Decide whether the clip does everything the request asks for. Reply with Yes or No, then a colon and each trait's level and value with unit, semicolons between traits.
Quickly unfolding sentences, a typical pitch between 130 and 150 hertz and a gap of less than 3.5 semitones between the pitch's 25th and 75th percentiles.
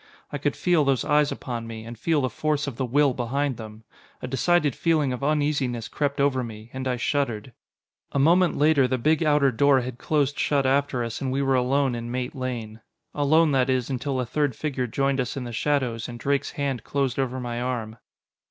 Yes: fast, 210 wpm; low, 135 Hz; average, 2.8 semitones